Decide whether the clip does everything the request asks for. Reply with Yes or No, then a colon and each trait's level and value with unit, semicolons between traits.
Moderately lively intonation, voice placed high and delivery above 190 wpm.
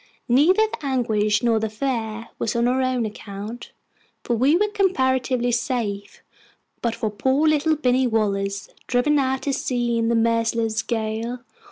No: average, 3.0 semitones; high, 240 Hz; average, 155 wpm